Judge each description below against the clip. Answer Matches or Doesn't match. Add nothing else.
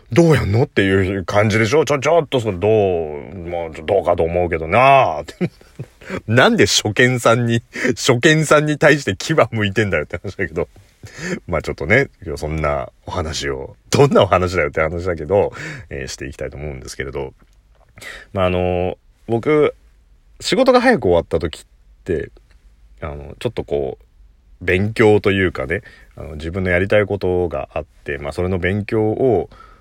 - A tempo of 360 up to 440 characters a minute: Doesn't match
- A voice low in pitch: Matches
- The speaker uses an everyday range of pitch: Doesn't match